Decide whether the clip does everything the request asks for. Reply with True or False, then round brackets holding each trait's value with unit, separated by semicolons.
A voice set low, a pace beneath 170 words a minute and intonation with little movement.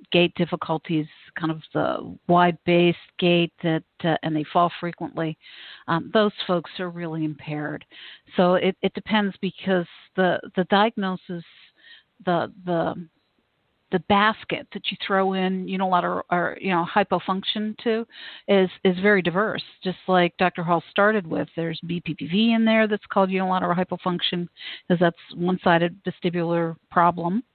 False (180 Hz; 145 wpm; 2.2 semitones)